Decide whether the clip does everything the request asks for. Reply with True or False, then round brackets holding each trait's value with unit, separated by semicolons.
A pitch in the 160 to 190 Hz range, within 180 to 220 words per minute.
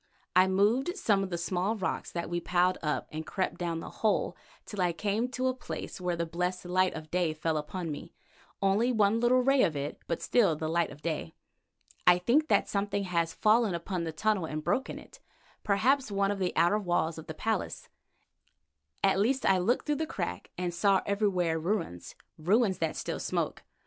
True (185 Hz; 195 wpm)